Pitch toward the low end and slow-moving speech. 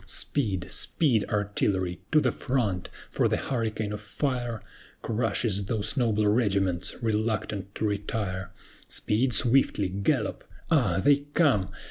Yes: low, 105 Hz; slow, 120 wpm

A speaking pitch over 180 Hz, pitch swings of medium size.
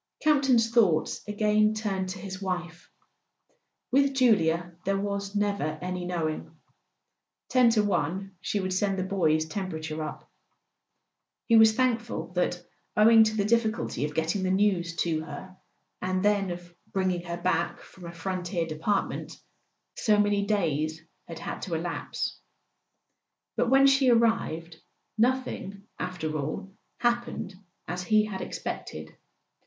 Yes: high, 190 Hz; average, 3.8 semitones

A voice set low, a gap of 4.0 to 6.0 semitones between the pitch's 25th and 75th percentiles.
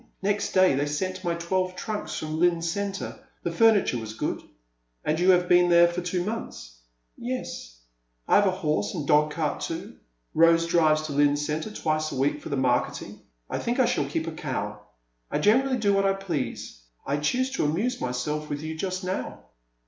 No: medium, 170 Hz; average, 4.3 semitones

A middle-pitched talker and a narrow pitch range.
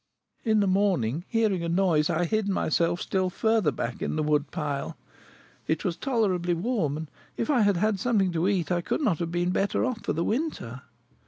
No: medium, 180 Hz; average, 4.6 semitones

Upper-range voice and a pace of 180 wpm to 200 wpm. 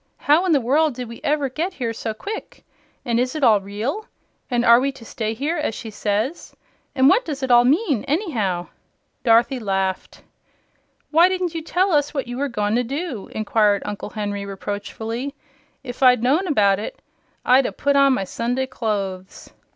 Yes: very high, 250 Hz; average, 185 wpm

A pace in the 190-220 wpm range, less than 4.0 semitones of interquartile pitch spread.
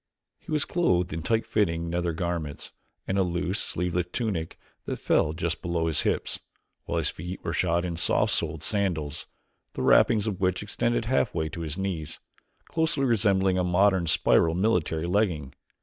No: average, 165 wpm; average, 3.4 semitones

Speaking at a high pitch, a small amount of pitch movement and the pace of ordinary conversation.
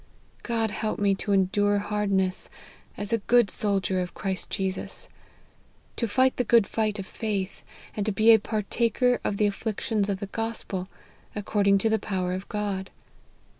Yes: high, 205 Hz; narrow, 2.2 semitones; average, 165 wpm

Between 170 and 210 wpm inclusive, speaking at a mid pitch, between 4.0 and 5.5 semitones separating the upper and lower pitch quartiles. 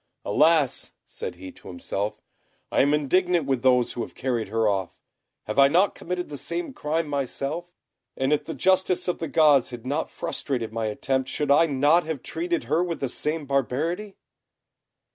Yes: average, 180 wpm; medium, 145 Hz; average, 4.8 semitones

